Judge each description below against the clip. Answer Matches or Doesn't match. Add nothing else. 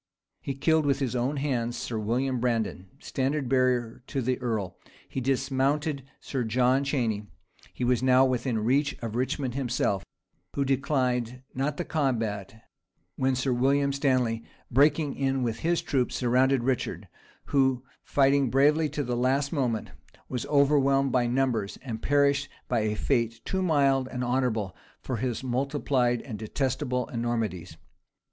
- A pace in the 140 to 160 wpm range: Matches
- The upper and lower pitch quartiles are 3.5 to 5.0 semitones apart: Doesn't match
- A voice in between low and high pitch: Doesn't match